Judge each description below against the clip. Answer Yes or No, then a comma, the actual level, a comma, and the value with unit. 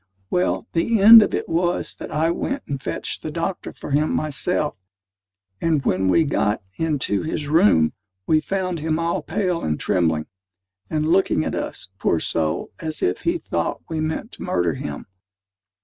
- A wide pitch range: Yes, wide, 5.7 semitones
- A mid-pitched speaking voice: Yes, medium, 155 Hz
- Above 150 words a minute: Yes, average, 170 wpm